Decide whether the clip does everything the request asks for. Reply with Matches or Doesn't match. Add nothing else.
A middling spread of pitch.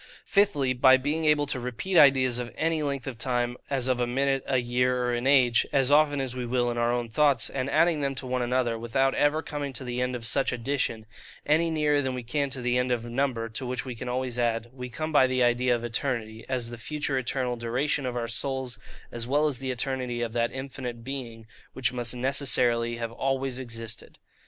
Doesn't match